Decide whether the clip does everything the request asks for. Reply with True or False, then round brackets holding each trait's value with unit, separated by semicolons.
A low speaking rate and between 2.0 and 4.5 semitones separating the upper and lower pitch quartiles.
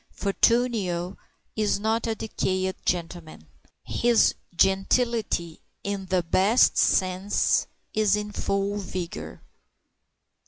True (90 wpm; 2.9 semitones)